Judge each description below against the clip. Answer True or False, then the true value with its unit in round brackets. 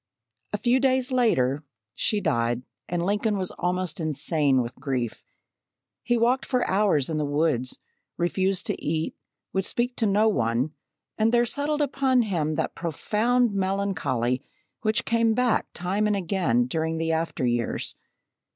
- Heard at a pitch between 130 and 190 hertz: True (185 Hz)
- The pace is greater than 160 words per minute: False (150 wpm)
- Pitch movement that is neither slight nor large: False (7.2 semitones)